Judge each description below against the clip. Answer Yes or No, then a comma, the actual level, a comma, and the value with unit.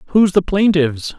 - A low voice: No, medium, 175 Hz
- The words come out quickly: No, average, 150 wpm